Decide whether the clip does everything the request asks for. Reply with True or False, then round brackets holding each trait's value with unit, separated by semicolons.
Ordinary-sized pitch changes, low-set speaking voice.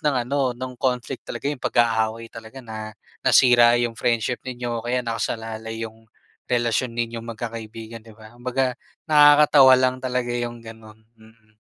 False (2.0 semitones; 120 Hz)